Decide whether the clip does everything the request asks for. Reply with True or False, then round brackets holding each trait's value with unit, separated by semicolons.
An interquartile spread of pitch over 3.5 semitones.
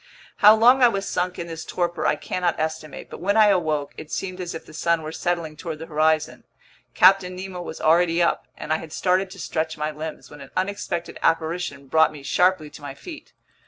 False (2.8 semitones)